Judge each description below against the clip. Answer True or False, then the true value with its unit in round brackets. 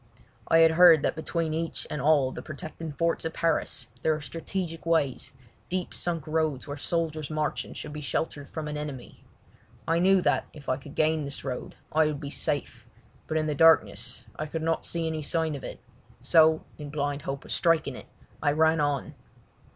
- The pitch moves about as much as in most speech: False (2.0 semitones)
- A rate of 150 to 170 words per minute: False (195 wpm)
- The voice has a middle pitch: True (155 Hz)